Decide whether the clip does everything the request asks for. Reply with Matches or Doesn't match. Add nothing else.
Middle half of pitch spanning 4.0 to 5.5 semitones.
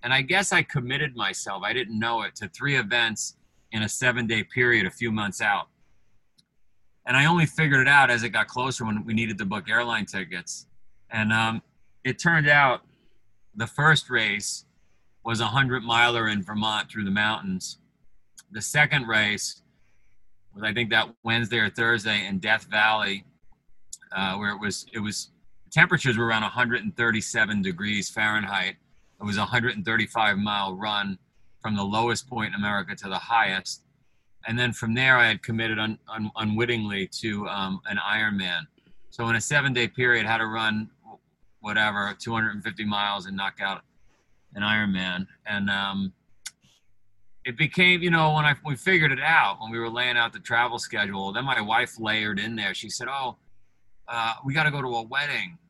Doesn't match